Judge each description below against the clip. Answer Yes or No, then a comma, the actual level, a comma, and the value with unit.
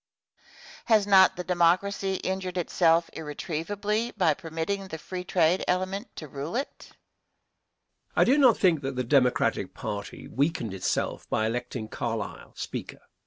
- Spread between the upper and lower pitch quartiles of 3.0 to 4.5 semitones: No, average, 5.1 semitones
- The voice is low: No, medium, 175 Hz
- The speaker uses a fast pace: No, average, 140 wpm